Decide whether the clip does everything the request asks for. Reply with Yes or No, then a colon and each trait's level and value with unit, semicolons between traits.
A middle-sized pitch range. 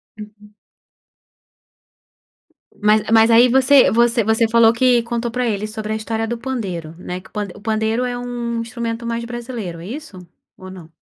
No: narrow, 2.1 semitones